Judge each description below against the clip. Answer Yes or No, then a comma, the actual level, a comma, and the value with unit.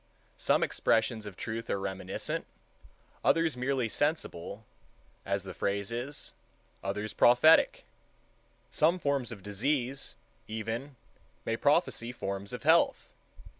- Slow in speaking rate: Yes, slow, 100 wpm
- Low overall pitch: Yes, low, 115 Hz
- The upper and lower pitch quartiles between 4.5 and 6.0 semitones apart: Yes, average, 5.3 semitones